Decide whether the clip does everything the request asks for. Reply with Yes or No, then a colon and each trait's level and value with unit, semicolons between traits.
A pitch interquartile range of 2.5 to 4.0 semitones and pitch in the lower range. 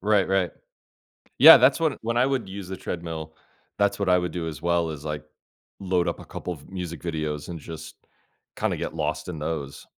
Yes: average, 3.5 semitones; very low, 85 Hz